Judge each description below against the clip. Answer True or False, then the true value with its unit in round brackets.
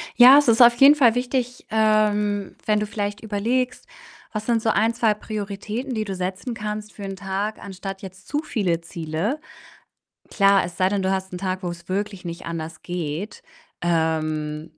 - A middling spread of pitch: True (3.3 semitones)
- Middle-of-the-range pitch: False (205 Hz)